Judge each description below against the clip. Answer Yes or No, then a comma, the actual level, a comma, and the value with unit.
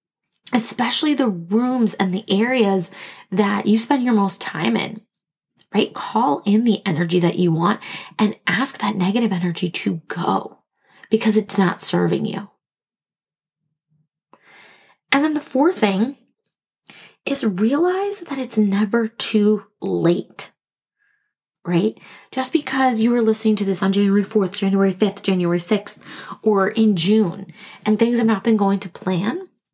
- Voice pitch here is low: No, high, 210 Hz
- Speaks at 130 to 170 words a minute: Yes, average, 145 wpm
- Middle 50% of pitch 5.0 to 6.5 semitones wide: No, average, 3.4 semitones